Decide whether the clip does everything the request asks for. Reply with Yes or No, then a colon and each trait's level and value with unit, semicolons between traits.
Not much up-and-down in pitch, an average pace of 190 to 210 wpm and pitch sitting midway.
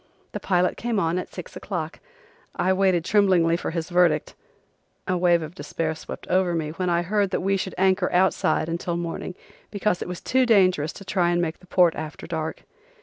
Yes: narrow, 2.2 semitones; average, 200 wpm; medium, 180 Hz